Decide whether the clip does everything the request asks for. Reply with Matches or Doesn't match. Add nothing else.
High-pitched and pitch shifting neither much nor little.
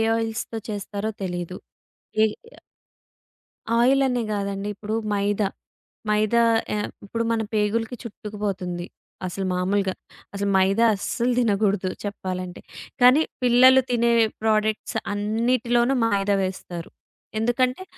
Matches